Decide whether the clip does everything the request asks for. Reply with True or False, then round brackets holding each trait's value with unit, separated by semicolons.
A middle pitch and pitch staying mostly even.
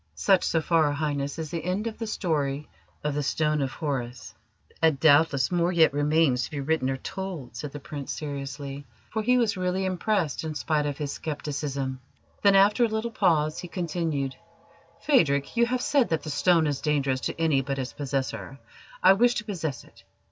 False (155 Hz; 4.5 semitones)